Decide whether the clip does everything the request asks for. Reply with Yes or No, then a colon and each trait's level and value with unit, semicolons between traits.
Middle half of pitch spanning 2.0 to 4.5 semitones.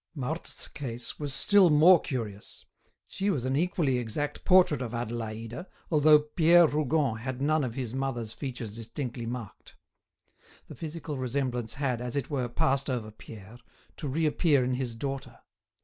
Yes: average, 4.1 semitones